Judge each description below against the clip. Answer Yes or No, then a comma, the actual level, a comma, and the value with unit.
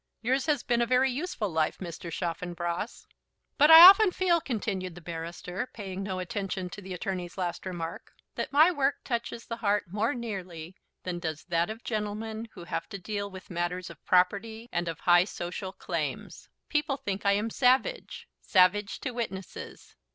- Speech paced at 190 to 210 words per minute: No, average, 175 wpm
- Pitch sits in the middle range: No, high, 200 Hz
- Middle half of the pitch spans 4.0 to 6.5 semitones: Yes, average, 4.9 semitones